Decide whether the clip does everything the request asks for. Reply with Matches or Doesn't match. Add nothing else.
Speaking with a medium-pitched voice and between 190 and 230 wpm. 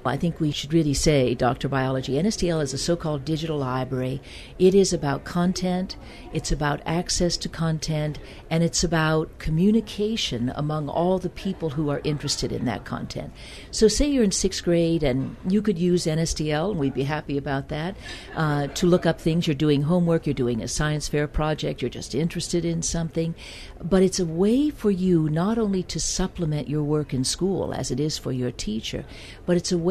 Matches